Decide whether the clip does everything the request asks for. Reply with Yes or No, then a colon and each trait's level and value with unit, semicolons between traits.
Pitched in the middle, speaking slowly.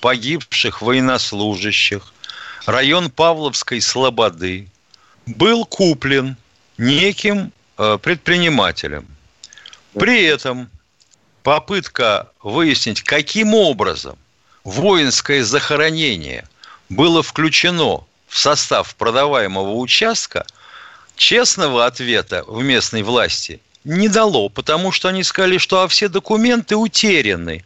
Yes: medium, 150 Hz; slow, 85 wpm